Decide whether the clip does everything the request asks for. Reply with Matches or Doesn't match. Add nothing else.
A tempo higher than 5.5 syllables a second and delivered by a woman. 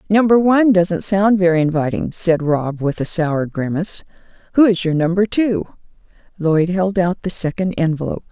Doesn't match